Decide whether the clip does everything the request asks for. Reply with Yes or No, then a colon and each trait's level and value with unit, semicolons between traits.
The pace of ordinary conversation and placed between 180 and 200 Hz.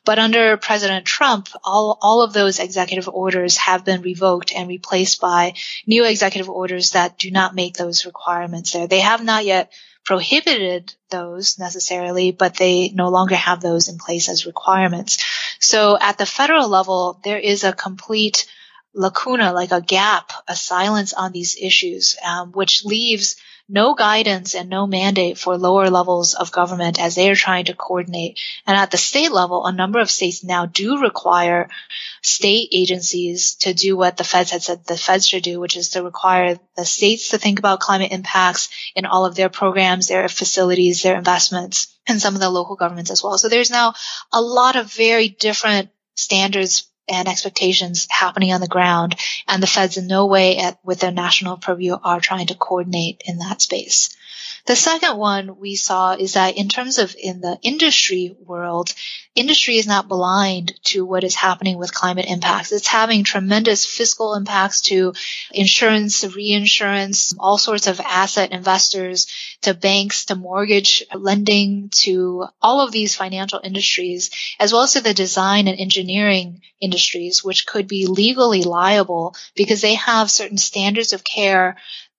Yes: average, 175 wpm; high, 190 Hz